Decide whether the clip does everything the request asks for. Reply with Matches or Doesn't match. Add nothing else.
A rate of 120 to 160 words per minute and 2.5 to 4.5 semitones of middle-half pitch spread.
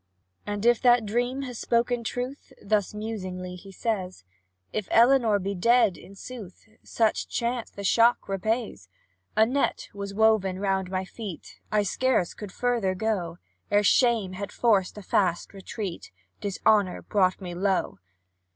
Matches